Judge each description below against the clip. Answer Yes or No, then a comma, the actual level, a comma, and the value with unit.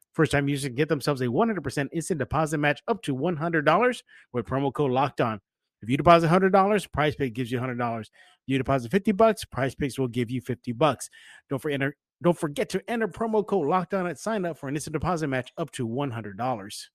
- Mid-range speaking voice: Yes, medium, 150 Hz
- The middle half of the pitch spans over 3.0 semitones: Yes, wide, 5.5 semitones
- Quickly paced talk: Yes, fast, 210 wpm